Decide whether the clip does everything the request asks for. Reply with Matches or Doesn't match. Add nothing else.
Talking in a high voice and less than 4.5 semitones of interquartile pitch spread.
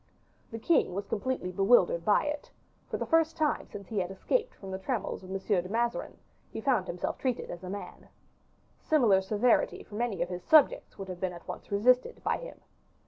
Doesn't match